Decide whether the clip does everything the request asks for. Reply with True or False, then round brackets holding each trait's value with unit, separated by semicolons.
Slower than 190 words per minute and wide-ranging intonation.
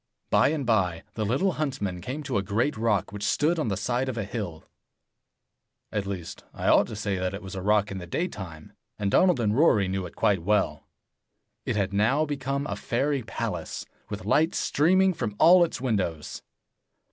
False (195 wpm; 6.4 semitones)